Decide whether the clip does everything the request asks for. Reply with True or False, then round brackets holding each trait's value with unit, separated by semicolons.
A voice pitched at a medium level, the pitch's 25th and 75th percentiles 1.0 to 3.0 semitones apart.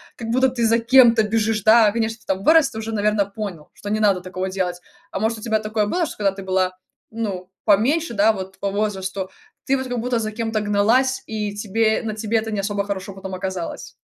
False (215 Hz; 2.6 semitones)